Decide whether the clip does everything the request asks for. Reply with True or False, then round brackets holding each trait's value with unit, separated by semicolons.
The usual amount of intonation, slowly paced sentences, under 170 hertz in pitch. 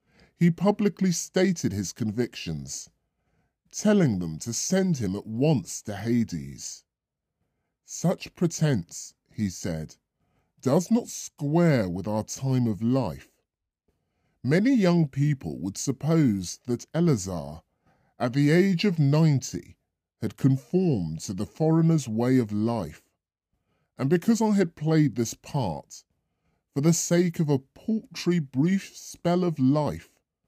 False (8.2 semitones; 125 wpm; 135 Hz)